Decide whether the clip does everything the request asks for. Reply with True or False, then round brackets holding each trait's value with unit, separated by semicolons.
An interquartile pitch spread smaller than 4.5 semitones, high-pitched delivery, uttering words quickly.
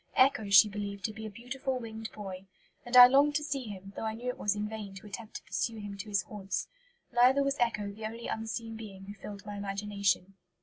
True (3.0 semitones; 215 Hz; 230 wpm)